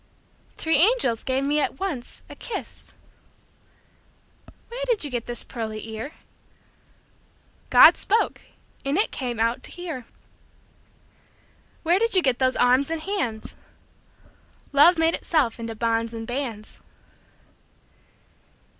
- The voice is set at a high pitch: Yes, very high, 270 Hz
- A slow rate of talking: Yes, slow, 110 wpm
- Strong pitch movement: Yes, wide, 6.2 semitones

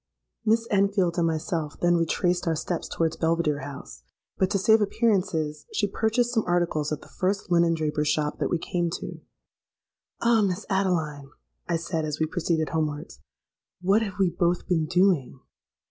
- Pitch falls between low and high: Yes, medium, 175 Hz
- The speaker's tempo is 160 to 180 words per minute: Yes, average, 165 wpm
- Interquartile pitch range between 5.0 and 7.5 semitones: No, average, 3.7 semitones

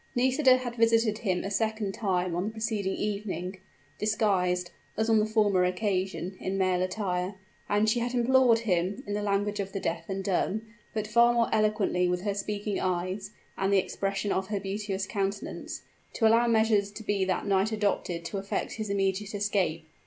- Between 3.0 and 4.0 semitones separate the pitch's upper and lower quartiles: No, narrow, 2.4 semitones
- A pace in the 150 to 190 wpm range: Yes, average, 180 wpm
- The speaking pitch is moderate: No, high, 200 Hz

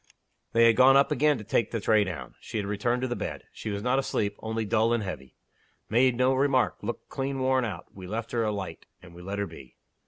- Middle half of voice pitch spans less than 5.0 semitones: Yes, average, 4.0 semitones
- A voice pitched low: Yes, low, 115 Hz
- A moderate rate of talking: No, fast, 245 wpm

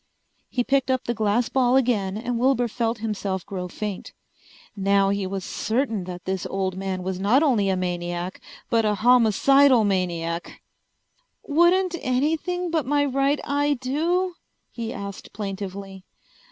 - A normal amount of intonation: No, wide, 5.9 semitones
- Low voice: No, high, 225 Hz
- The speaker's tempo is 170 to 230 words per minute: No, average, 145 wpm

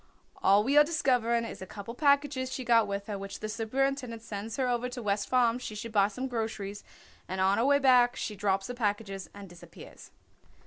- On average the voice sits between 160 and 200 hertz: No, high, 230 Hz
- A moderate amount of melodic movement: Yes, average, 3.9 semitones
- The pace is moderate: No, fast, 210 wpm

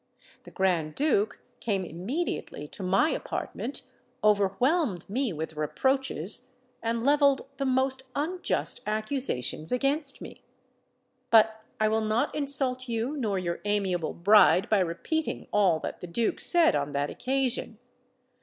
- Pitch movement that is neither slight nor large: No, wide, 6.4 semitones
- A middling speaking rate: No, slow, 130 wpm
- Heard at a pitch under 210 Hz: No, high, 220 Hz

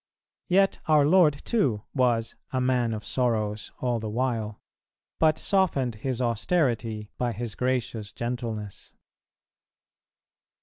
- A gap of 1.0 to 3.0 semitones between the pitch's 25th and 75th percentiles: No, average, 3.5 semitones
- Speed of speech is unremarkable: No, slow, 115 wpm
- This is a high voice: No, low, 120 Hz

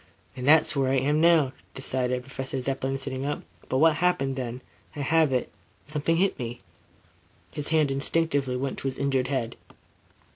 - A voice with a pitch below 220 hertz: Yes, low, 135 Hz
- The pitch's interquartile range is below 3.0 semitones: Yes, narrow, 2.5 semitones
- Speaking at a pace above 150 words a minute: Yes, average, 170 wpm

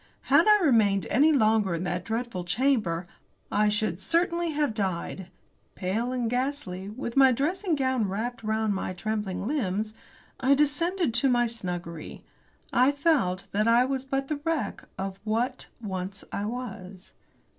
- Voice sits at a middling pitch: No, high, 230 Hz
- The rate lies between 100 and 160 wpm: Yes, average, 150 wpm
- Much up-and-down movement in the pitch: Yes, wide, 5.8 semitones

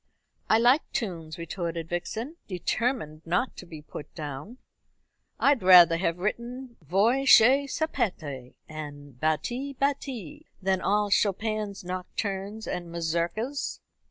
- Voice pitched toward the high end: Yes, high, 195 Hz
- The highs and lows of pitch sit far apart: Yes, wide, 6.3 semitones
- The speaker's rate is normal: No, slow, 115 wpm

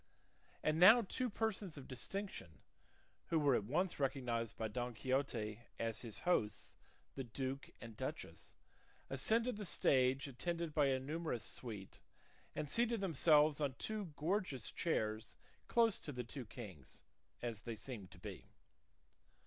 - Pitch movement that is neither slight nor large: No, wide, 6.5 semitones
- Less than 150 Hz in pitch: Yes, low, 135 Hz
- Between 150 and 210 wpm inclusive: No, average, 140 wpm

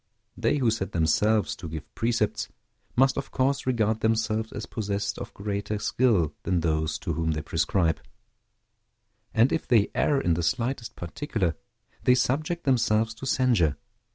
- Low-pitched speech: Yes, low, 110 Hz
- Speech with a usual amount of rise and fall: No, wide, 5.8 semitones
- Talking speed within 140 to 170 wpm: Yes, average, 155 wpm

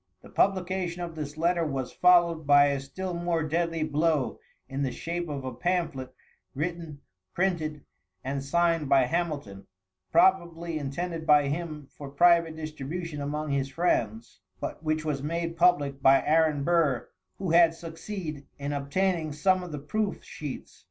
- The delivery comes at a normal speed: Yes, average, 150 wpm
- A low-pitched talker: No, medium, 155 Hz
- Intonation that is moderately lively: Yes, average, 3.3 semitones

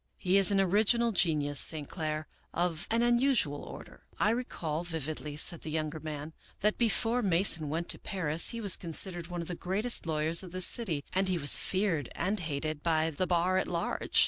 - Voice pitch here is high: No, medium, 175 Hz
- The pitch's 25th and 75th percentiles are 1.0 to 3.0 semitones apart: No, average, 4.0 semitones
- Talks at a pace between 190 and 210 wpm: Yes, average, 200 wpm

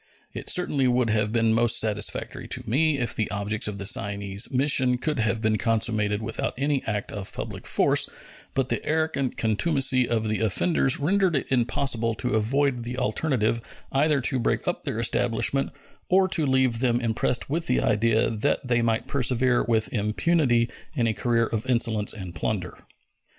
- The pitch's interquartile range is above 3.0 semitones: Yes, average, 3.5 semitones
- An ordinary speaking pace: Yes, average, 170 wpm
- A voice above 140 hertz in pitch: No, low, 120 Hz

